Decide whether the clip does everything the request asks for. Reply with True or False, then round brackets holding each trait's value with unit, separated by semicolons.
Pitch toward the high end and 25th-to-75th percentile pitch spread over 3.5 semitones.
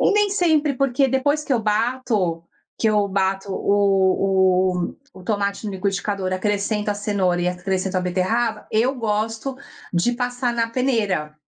True (205 Hz; 4.3 semitones)